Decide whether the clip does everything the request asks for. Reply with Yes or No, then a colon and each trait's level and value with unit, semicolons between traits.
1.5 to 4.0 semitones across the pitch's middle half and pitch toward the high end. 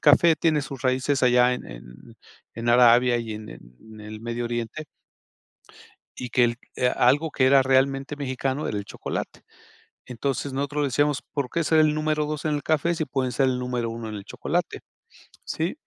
No: average, 3.7 semitones; low, 130 Hz